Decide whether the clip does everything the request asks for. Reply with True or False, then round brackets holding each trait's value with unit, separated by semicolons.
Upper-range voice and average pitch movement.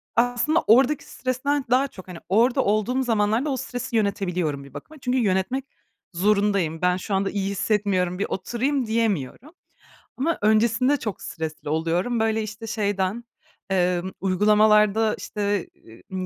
True (210 Hz; 4.4 semitones)